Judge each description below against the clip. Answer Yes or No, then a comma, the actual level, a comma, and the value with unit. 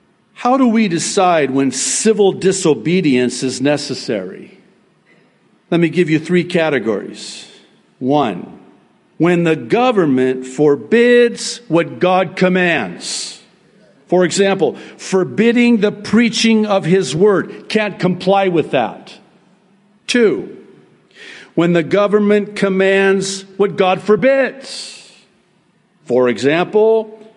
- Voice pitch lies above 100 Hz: Yes, high, 190 Hz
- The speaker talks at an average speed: No, slow, 100 wpm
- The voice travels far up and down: No, average, 3.7 semitones